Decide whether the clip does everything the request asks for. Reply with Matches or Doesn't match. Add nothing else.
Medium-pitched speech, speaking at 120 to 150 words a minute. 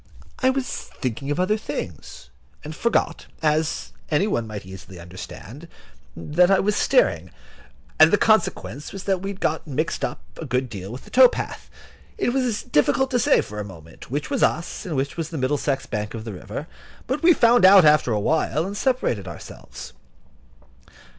Doesn't match